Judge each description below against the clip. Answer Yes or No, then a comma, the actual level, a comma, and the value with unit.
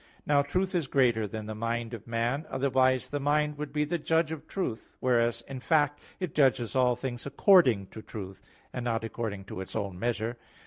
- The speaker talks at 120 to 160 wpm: No, average, 195 wpm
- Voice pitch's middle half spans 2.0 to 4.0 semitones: No, average, 4.4 semitones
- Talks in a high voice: No, low, 125 Hz